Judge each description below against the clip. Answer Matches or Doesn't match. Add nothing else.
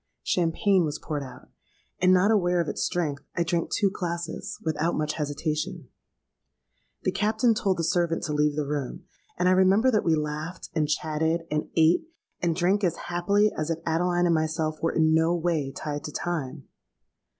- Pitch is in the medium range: Matches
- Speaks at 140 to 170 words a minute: Doesn't match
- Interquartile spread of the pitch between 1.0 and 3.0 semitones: Matches